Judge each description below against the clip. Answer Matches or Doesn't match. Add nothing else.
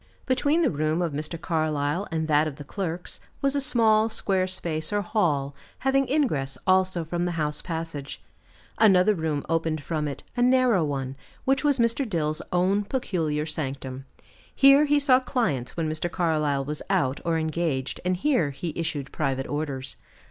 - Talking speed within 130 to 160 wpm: Doesn't match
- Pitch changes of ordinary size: Doesn't match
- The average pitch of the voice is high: Doesn't match